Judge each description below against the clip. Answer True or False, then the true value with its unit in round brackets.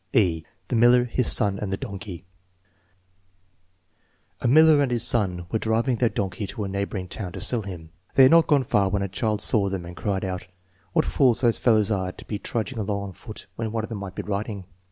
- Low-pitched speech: True (105 Hz)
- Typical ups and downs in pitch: True (3.3 semitones)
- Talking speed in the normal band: False (225 wpm)